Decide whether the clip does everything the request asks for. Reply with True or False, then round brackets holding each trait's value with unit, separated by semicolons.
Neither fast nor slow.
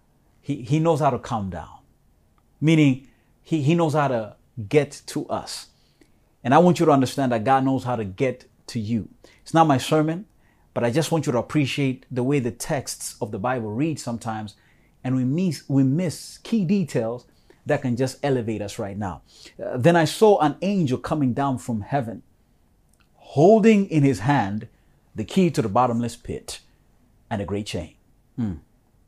True (185 wpm)